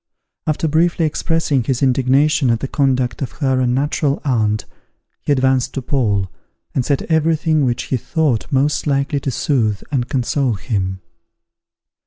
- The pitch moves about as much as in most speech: Yes, average, 3.2 semitones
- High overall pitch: No, low, 135 Hz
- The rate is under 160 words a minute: Yes, average, 150 wpm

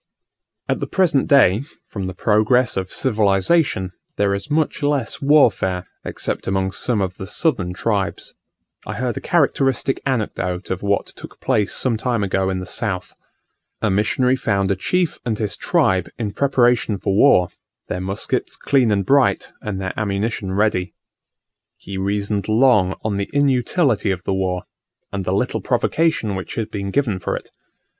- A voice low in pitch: Yes, low, 105 Hz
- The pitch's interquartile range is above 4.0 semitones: Yes, average, 5.1 semitones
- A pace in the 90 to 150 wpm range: No, average, 165 wpm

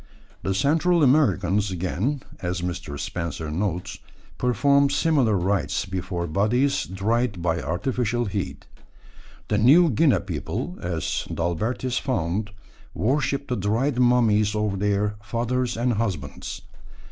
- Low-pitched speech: Yes, low, 105 Hz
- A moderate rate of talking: No, slow, 115 wpm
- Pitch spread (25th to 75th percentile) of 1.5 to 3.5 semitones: No, wide, 5.6 semitones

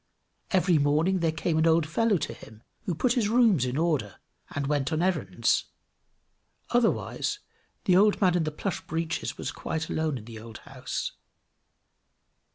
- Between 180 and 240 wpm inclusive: No, average, 165 wpm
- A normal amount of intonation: Yes, average, 4.5 semitones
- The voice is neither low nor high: Yes, medium, 160 Hz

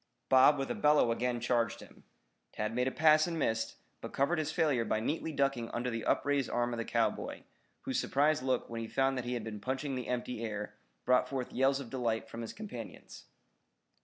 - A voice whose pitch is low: Yes, low, 125 Hz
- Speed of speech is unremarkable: No, fast, 210 wpm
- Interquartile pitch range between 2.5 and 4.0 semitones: Yes, average, 3.3 semitones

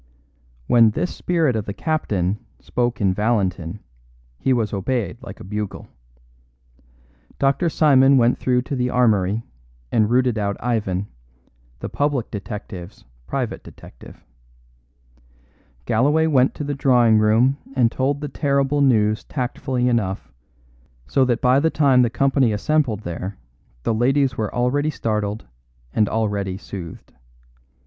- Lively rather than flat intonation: No, average, 4.4 semitones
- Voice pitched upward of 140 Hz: No, low, 120 Hz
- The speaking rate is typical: No, slow, 130 wpm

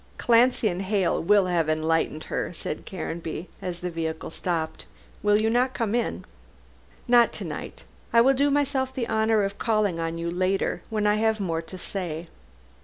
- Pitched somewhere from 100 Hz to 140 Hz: No, high, 195 Hz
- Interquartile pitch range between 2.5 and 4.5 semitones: No, wide, 5.4 semitones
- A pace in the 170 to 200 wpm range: Yes, average, 175 wpm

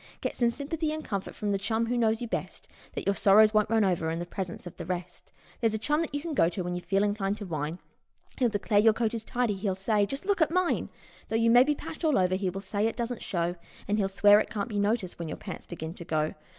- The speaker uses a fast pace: Yes, fast, 280 wpm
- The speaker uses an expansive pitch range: No, average, 4.0 semitones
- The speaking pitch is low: No, high, 210 Hz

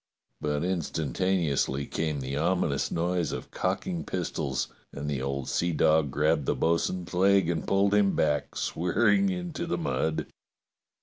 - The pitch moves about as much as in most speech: Yes, average, 4.4 semitones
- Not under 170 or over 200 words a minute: No, average, 145 wpm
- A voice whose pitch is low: Yes, very low, 85 Hz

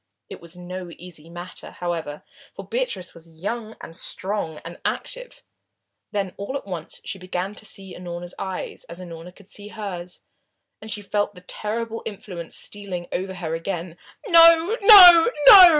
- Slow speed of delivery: No, average, 160 wpm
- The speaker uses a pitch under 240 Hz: Yes, medium, 185 Hz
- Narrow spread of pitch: No, average, 3.8 semitones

